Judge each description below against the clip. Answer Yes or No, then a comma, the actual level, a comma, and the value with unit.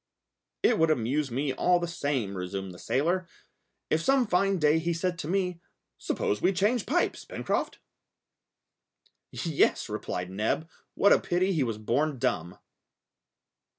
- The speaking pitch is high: No, medium, 155 Hz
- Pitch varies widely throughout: Yes, wide, 7.5 semitones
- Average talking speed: Yes, average, 145 wpm